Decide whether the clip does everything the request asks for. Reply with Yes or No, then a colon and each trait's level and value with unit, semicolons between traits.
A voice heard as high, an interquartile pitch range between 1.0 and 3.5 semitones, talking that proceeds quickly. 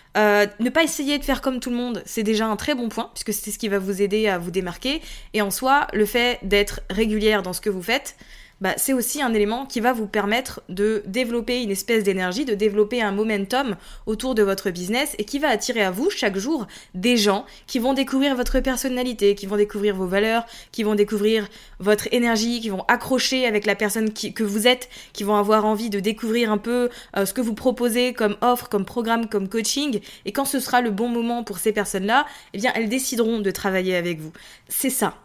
Yes: high, 220 Hz; average, 3.1 semitones; fast, 230 wpm